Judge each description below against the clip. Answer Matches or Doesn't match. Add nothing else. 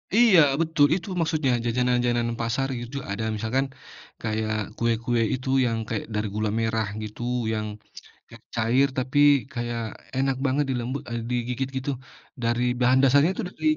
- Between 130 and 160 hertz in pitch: Doesn't match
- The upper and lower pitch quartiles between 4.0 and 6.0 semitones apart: Doesn't match